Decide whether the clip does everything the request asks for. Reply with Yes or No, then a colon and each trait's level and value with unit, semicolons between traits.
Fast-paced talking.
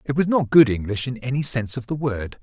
Yes: fast, 270 wpm